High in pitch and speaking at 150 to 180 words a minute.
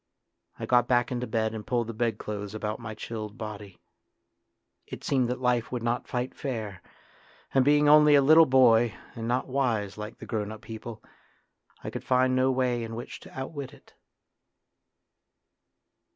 No: low, 120 Hz; average, 165 wpm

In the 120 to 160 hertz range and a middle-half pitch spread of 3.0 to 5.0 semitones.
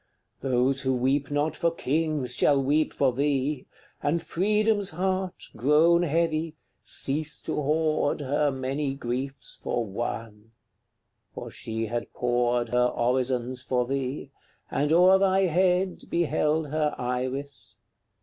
Yes: medium, 140 Hz; average, 4.1 semitones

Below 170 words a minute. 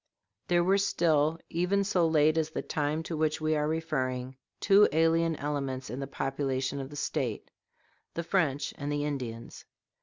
No: average, 175 wpm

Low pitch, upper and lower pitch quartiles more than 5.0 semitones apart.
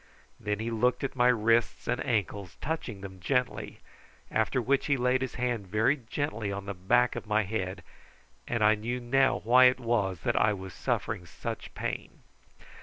No: low, 115 Hz; average, 3.7 semitones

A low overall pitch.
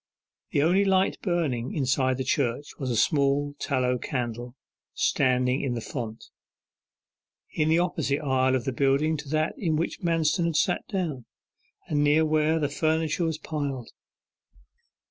No: medium, 145 Hz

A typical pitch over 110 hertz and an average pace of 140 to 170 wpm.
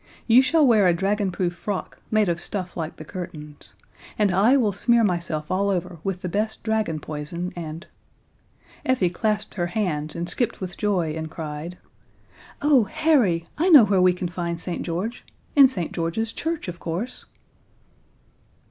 Yes: medium, 185 Hz; average, 165 wpm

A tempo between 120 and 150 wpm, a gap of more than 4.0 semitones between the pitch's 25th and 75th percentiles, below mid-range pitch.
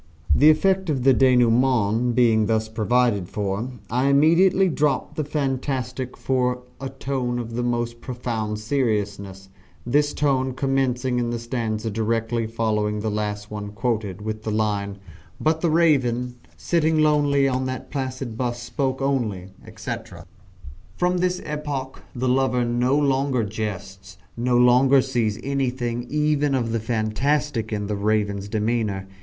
No: average, 140 wpm; average, 3.7 semitones; low, 125 Hz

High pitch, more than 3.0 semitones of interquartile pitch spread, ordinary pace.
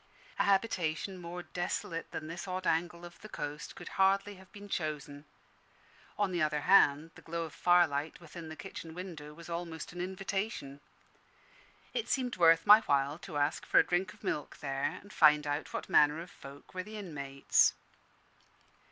No: medium, 170 Hz; average, 3.8 semitones; average, 175 wpm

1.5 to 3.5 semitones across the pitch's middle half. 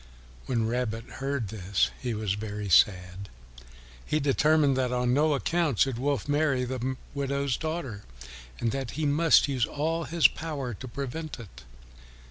No: average, 4.3 semitones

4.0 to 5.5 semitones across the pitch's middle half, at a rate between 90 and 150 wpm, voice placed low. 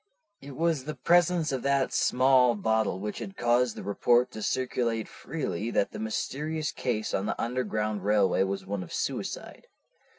No: average, 4.4 semitones; average, 165 wpm; low, 120 Hz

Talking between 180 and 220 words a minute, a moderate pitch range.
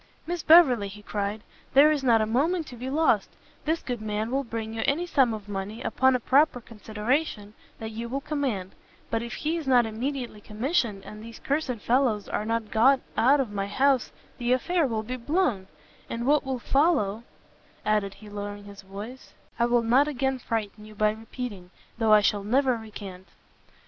Yes: average, 190 wpm; average, 4.2 semitones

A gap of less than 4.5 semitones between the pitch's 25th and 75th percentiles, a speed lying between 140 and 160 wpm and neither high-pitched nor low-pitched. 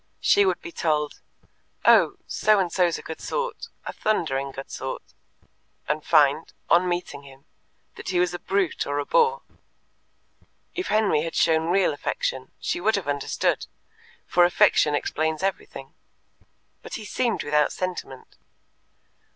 No: average, 5.1 semitones; average, 145 wpm; medium, 170 Hz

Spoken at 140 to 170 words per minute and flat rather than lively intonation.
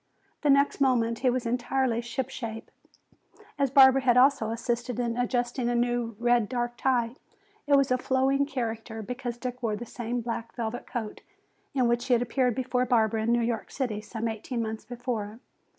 No: average, 185 wpm; narrow, 1.8 semitones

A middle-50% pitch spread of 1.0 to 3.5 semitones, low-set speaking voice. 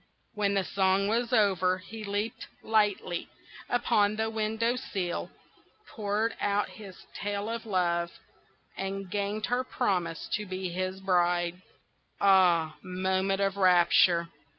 No: average, 2.7 semitones; high, 195 Hz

